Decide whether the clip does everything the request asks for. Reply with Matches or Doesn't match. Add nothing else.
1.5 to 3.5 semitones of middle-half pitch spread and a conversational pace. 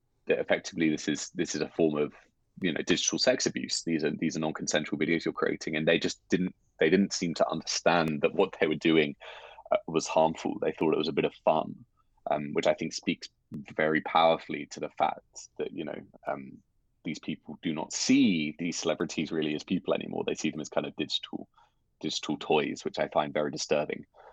Matches